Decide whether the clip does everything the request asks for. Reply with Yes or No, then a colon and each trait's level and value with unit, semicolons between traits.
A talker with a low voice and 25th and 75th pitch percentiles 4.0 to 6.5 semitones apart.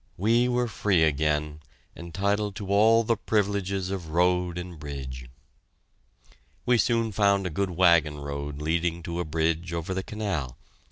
Yes: very low, 90 Hz; average, 4.5 semitones